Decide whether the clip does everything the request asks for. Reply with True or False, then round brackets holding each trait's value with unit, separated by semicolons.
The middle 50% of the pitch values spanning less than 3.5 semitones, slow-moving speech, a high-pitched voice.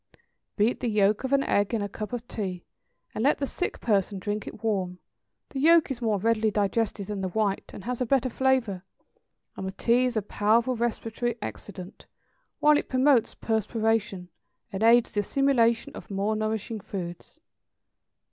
False (3.1 semitones; 175 wpm; 220 Hz)